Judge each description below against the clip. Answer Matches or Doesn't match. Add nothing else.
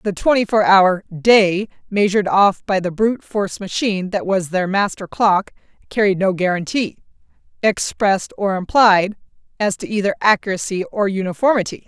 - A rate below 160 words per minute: Matches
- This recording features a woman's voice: Matches